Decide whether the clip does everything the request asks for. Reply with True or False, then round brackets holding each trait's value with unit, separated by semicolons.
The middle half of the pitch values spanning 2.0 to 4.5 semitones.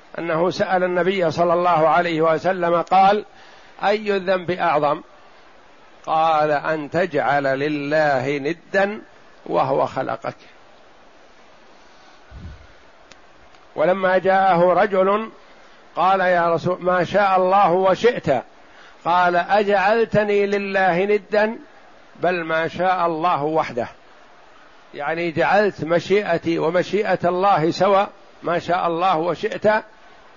True (3.0 semitones)